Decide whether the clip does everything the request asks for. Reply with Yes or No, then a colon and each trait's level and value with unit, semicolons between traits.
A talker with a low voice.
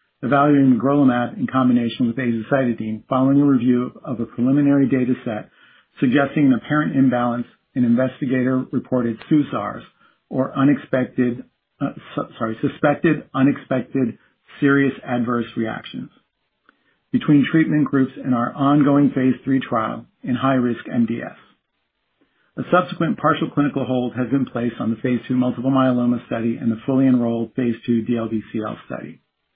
Yes: low, 130 Hz